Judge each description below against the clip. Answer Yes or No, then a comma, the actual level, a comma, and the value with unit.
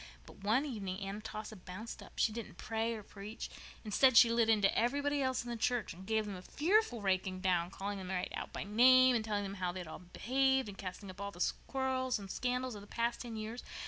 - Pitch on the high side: Yes, high, 215 Hz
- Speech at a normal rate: No, fast, 240 wpm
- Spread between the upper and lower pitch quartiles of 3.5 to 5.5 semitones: Yes, average, 4.1 semitones